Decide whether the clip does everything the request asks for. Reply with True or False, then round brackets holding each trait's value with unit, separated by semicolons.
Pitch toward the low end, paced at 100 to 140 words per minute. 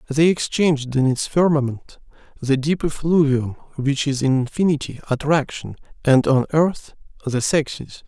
False (145 Hz; 135 wpm)